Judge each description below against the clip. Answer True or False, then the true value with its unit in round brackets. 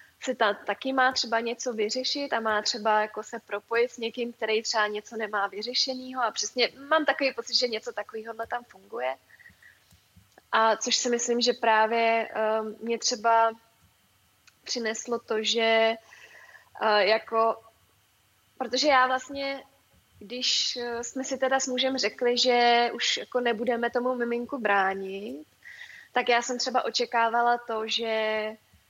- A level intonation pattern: True (2.3 semitones)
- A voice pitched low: False (230 Hz)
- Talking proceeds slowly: False (135 wpm)